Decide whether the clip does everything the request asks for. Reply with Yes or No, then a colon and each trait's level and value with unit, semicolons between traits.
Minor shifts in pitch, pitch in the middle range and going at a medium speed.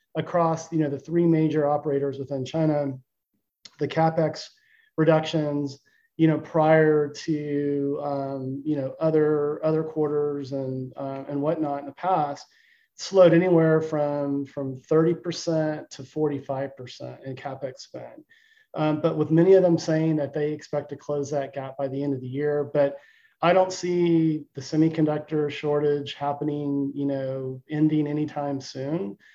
Yes: narrow, 2.2 semitones; medium, 150 Hz; average, 145 wpm